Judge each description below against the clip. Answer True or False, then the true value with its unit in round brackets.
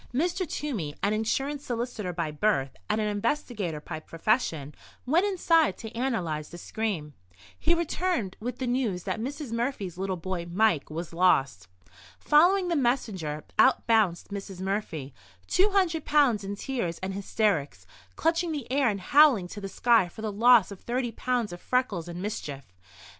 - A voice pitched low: False (215 Hz)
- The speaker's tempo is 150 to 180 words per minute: True (160 wpm)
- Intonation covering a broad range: True (7.1 semitones)